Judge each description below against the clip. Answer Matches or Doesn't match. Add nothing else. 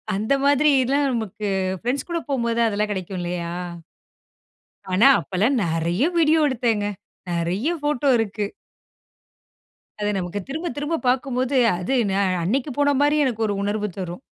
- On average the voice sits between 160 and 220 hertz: Doesn't match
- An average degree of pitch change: Doesn't match